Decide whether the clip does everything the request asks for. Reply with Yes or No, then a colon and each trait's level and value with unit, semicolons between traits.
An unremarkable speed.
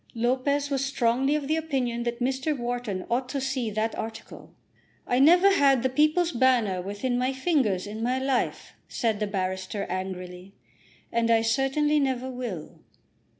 Yes: average, 155 wpm